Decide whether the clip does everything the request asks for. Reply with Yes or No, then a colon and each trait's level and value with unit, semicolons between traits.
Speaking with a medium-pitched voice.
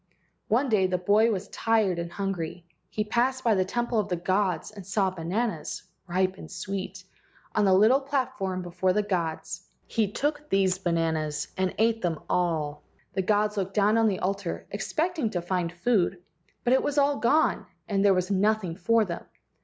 No: high, 195 Hz